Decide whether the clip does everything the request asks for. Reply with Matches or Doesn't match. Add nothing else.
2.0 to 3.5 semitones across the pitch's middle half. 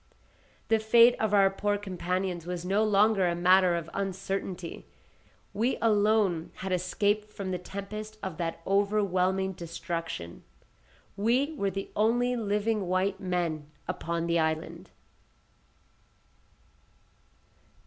Matches